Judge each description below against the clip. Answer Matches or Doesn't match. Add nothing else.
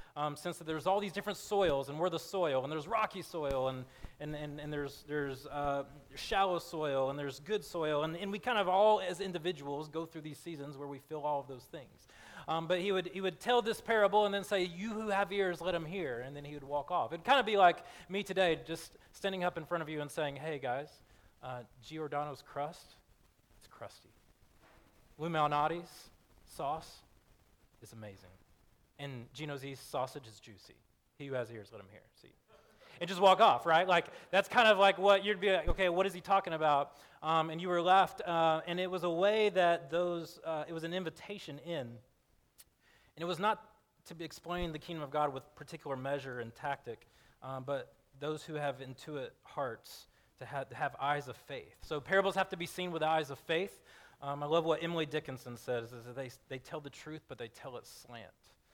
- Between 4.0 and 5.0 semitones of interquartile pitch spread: Matches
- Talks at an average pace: Doesn't match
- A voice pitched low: Doesn't match